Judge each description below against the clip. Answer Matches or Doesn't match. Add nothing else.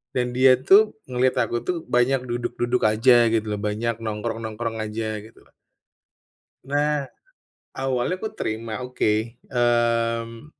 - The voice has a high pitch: Doesn't match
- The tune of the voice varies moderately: Doesn't match